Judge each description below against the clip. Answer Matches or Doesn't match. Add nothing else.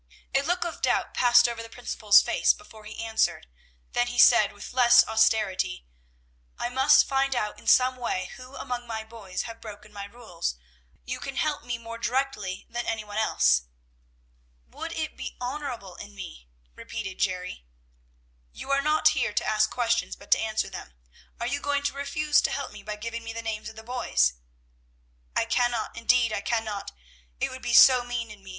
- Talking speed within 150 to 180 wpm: Doesn't match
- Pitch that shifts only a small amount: Doesn't match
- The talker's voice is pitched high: Matches